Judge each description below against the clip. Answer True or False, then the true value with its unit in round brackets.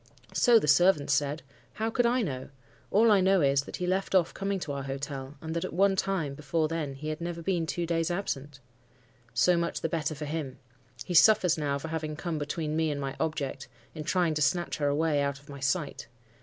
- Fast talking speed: True (220 wpm)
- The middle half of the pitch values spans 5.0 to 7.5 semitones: False (3.8 semitones)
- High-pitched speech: False (155 Hz)